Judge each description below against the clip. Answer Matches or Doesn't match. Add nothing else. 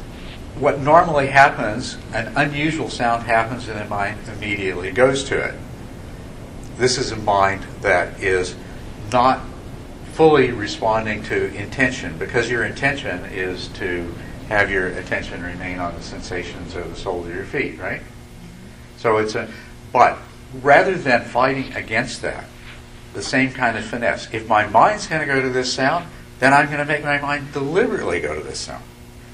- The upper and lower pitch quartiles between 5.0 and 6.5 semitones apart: Matches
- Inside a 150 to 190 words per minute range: Matches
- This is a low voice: Matches